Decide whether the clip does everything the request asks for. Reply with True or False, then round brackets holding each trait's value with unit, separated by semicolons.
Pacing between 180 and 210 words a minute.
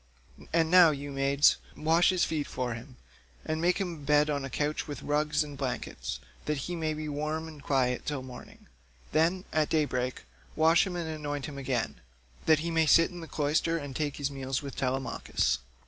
True (200 wpm)